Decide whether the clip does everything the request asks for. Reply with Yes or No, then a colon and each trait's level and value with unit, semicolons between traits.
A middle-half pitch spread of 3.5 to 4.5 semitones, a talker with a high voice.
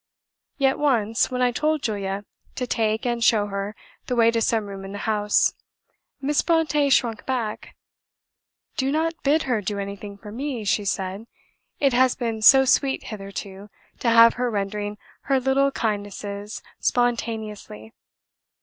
Yes: average, 4.1 semitones; high, 225 Hz